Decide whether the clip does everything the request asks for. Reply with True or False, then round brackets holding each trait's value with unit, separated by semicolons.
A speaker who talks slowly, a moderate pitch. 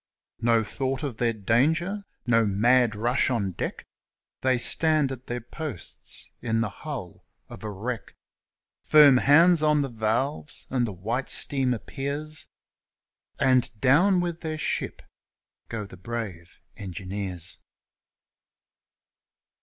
False (120 wpm; 125 Hz)